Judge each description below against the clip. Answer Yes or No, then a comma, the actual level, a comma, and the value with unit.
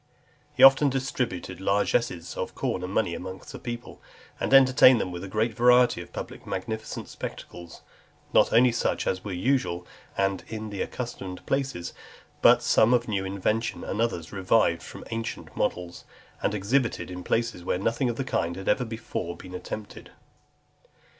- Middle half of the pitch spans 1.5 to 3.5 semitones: No, average, 4.7 semitones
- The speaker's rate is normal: Yes, average, 165 wpm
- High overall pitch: No, low, 105 Hz